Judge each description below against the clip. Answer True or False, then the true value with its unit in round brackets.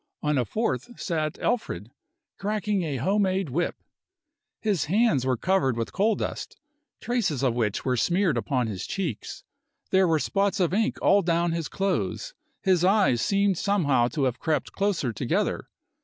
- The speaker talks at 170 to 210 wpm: False (160 wpm)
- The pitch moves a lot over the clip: True (7.1 semitones)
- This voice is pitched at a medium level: True (175 Hz)